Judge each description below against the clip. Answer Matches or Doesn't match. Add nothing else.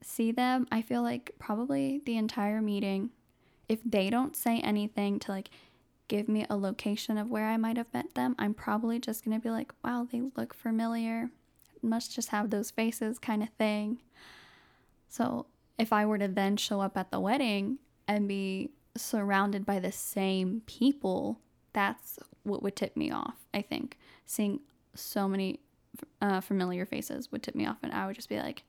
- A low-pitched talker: Doesn't match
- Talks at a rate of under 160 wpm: Doesn't match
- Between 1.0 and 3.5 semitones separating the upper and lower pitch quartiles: Matches